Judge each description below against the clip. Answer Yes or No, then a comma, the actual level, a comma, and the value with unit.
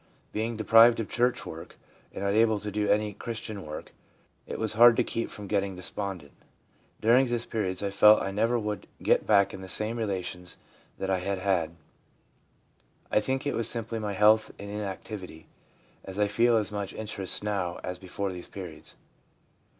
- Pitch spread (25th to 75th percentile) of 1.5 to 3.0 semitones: Yes, narrow, 2.6 semitones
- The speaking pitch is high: No, low, 105 Hz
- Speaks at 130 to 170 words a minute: No, average, 180 wpm